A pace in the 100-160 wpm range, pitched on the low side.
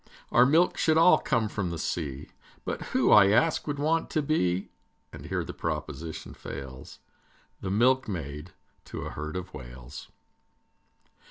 Yes: average, 150 wpm; very low, 95 Hz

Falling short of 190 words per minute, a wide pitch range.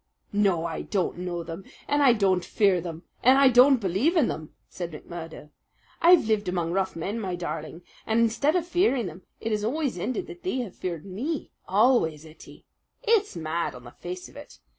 No: average, 195 wpm; wide, 7.2 semitones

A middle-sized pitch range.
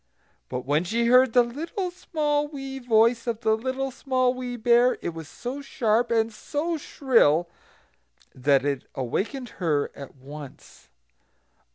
No: wide, 8.4 semitones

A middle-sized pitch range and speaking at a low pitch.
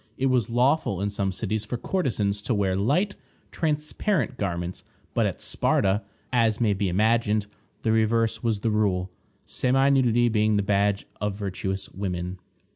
Yes: average, 3.4 semitones; low, 110 Hz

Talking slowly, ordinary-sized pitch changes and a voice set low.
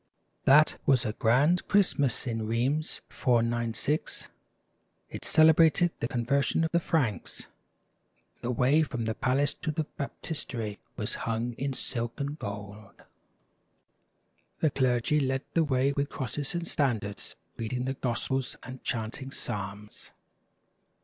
Yes: slow, 130 wpm; average, 4.0 semitones; low, 130 Hz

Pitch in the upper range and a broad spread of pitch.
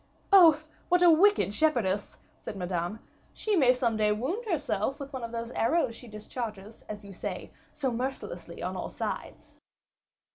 Yes: high, 245 Hz; wide, 6.5 semitones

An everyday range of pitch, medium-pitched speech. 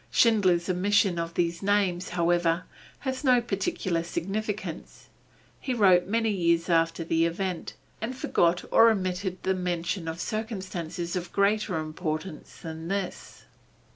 Yes: average, 3.2 semitones; medium, 180 Hz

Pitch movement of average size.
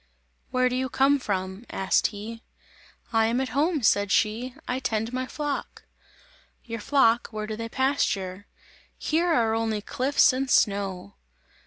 Yes: average, 3.7 semitones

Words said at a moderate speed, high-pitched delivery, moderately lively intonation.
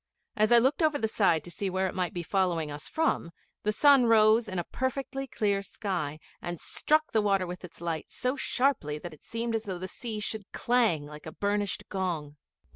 No: fast, 210 wpm; high, 200 Hz; average, 5.0 semitones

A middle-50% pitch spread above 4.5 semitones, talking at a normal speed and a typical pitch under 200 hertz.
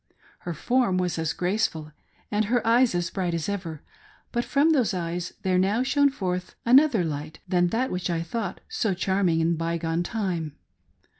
Yes: average, 5.3 semitones; average, 190 wpm; medium, 185 Hz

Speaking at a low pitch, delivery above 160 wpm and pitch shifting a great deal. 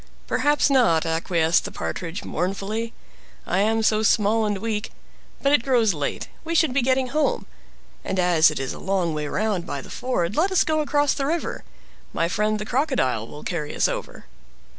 No: high, 215 Hz; average, 185 wpm; wide, 7.3 semitones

